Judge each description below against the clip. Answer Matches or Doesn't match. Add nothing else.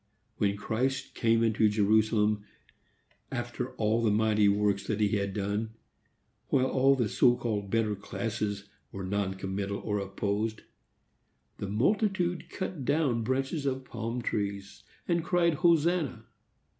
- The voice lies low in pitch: Matches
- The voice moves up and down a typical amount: Matches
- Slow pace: Matches